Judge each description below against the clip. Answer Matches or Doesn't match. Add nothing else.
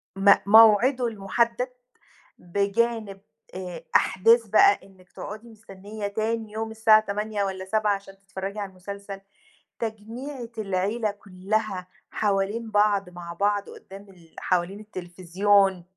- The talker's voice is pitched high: Matches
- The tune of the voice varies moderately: Doesn't match